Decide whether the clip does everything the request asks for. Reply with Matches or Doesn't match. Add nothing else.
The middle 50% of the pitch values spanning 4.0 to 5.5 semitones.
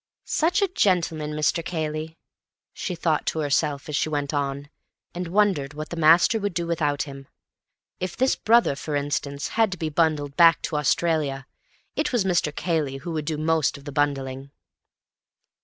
Doesn't match